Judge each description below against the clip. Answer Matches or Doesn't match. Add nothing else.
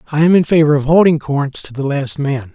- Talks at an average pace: Doesn't match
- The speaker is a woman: Doesn't match